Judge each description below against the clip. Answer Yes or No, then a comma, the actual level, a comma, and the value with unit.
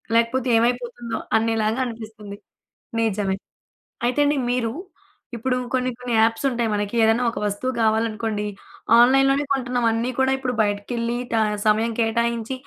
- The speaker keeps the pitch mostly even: Yes, narrow, 2.1 semitones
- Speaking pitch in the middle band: No, high, 230 Hz